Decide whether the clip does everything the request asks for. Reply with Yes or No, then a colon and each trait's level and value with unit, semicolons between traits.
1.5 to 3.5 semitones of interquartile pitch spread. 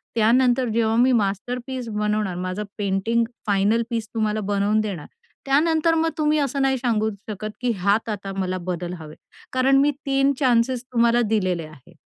No: average, 4.2 semitones